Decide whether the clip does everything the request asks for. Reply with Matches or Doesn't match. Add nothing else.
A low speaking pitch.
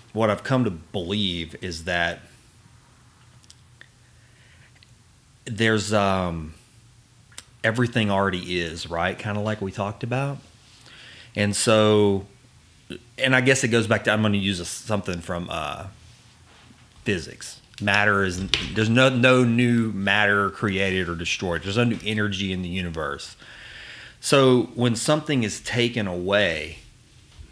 Matches